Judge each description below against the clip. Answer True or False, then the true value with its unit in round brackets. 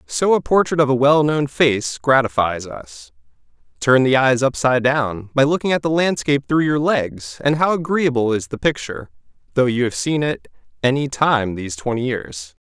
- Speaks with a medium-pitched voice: False (130 Hz)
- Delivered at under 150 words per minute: False (180 wpm)